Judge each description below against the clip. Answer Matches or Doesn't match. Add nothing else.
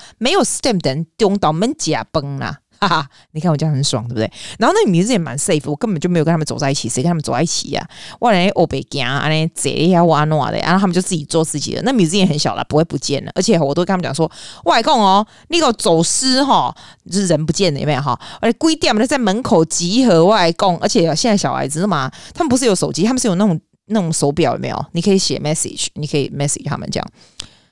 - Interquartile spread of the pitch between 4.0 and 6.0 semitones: Matches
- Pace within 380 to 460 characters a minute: Matches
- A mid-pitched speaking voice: Matches